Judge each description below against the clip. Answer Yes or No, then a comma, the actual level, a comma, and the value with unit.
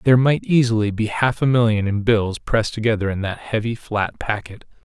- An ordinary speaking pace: Yes, average, 195 wpm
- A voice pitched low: Yes, low, 110 Hz